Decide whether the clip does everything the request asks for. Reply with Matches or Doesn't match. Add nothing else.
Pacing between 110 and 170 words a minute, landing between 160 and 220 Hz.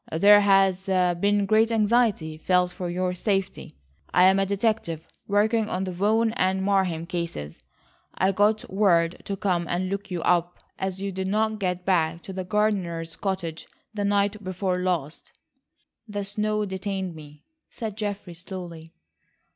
Matches